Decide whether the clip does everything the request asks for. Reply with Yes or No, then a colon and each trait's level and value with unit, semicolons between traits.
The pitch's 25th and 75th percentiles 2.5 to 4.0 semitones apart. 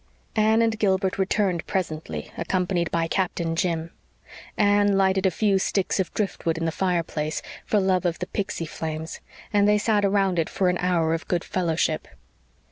Yes: average, 3.2 semitones